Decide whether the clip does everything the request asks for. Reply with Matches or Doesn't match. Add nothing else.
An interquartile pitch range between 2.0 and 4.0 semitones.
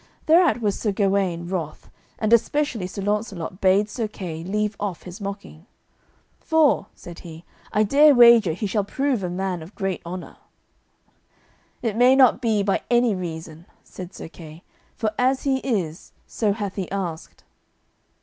Doesn't match